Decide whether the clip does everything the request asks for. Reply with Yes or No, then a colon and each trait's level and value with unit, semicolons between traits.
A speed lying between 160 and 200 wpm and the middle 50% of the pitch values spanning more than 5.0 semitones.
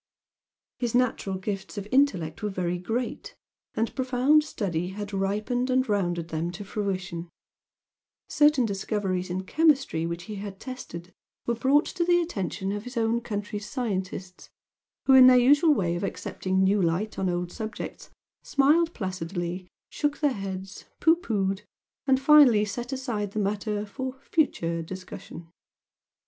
No: average, 145 wpm; wide, 5.5 semitones